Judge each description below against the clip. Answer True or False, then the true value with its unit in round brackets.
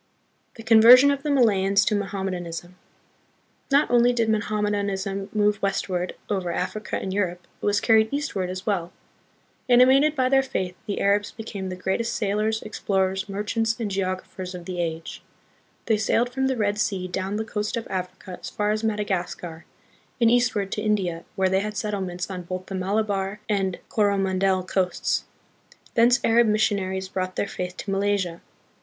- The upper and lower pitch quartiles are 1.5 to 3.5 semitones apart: True (2.7 semitones)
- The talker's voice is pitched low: False (200 Hz)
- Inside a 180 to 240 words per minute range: False (170 wpm)